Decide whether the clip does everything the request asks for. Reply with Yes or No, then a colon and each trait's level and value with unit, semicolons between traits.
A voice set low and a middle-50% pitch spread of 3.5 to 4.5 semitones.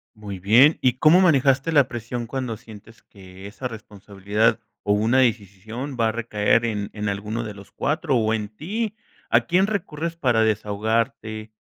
Yes: low, 115 Hz; average, 4.1 semitones